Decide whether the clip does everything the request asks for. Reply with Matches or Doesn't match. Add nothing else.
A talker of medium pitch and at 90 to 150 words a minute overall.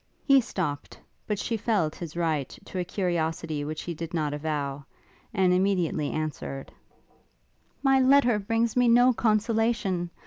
Matches